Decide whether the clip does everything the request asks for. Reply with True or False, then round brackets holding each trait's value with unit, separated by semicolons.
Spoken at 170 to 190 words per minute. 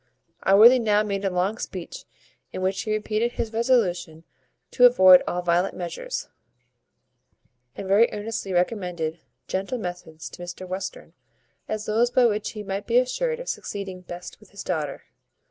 False (155 wpm)